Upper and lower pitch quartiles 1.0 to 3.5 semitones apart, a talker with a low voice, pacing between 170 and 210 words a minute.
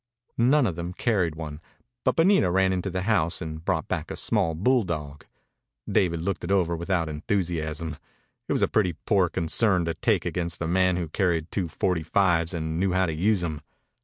Yes: average, 2.8 semitones; very low, 85 Hz; average, 190 wpm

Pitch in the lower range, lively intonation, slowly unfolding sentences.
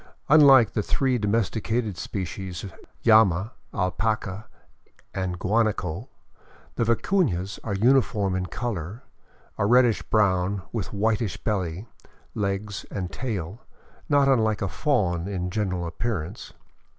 No: low, 105 Hz; average, 3.8 semitones; slow, 110 wpm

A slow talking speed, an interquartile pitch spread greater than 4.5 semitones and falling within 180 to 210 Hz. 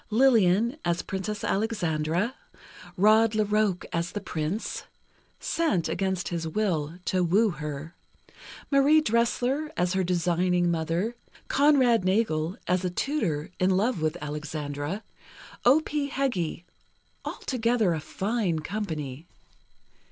Yes: slow, 115 wpm; wide, 5.6 semitones; high, 190 Hz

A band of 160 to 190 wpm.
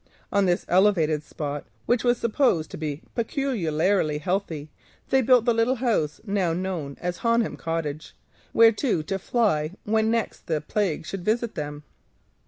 No: average, 145 wpm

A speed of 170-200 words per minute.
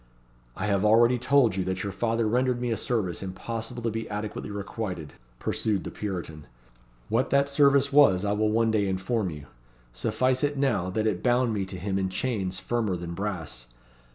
Yes: average, 185 wpm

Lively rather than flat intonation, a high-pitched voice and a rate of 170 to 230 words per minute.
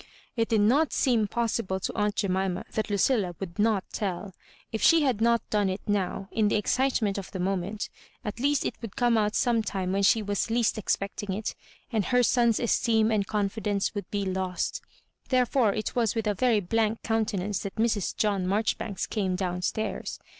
No: average, 2.7 semitones; high, 210 Hz; average, 195 wpm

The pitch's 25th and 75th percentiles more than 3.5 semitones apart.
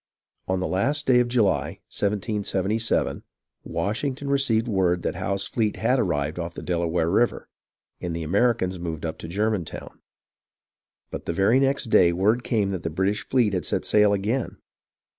Yes: average, 4.5 semitones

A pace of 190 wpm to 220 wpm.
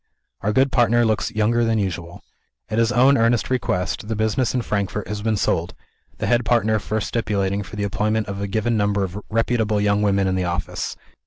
Yes: average, 200 wpm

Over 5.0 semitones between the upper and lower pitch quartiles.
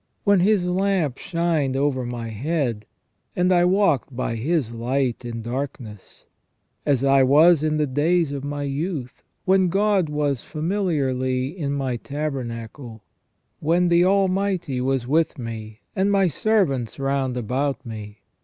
Yes: wide, 5.6 semitones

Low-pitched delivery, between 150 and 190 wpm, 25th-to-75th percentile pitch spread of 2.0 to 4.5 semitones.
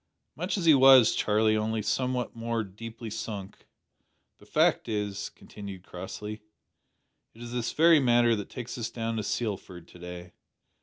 Yes: low, 110 Hz; average, 155 wpm; average, 2.8 semitones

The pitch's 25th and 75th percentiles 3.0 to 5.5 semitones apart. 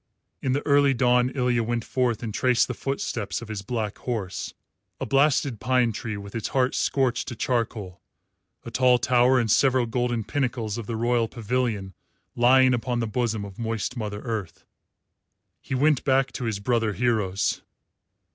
No: narrow, 2.6 semitones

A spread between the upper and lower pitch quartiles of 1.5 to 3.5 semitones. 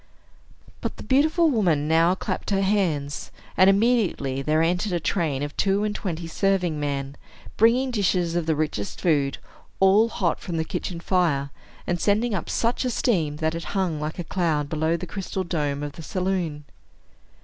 No: average, 4.3 semitones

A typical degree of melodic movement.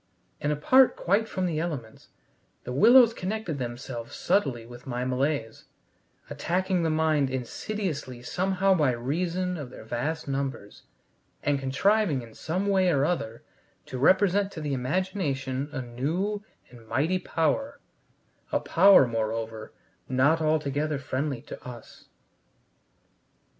No: wide, 6.3 semitones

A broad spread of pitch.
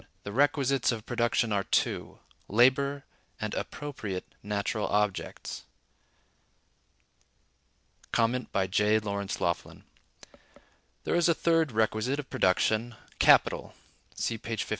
No: average, 4.6 semitones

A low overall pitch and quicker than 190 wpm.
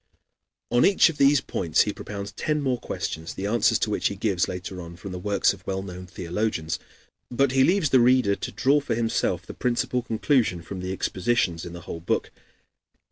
Yes: low, 100 Hz; average, 200 wpm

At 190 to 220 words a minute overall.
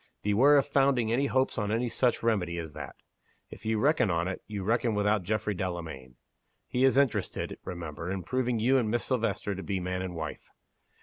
Yes: average, 195 wpm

